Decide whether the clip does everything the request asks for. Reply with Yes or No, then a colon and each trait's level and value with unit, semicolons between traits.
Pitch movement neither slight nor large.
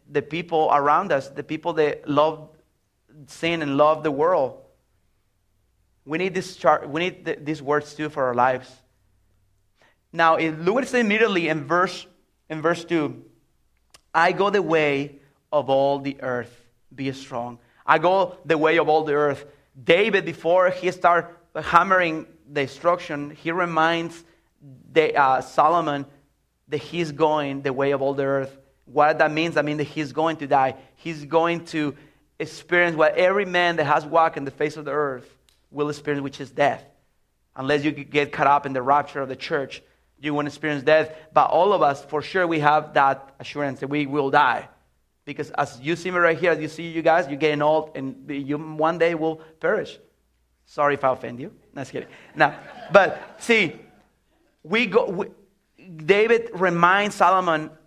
Yes: average, 3.0 semitones